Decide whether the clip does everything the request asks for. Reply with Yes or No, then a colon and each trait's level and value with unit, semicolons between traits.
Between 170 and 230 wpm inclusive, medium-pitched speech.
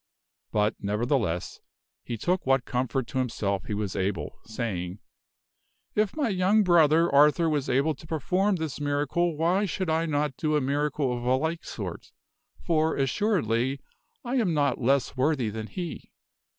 No: average, 155 wpm; medium, 145 Hz